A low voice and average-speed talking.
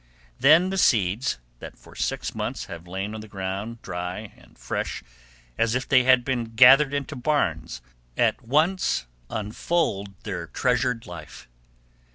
Yes: low, 115 Hz; average, 145 wpm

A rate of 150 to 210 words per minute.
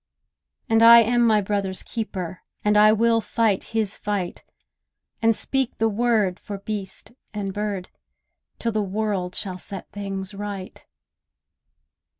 No: slow, 135 wpm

